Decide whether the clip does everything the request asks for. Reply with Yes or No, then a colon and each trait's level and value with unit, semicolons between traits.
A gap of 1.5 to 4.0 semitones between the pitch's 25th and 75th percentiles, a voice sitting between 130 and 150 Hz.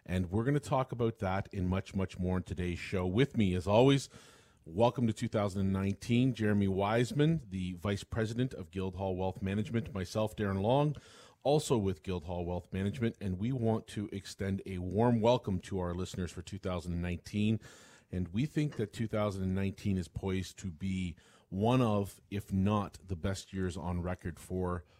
No: average, 3.5 semitones; low, 100 Hz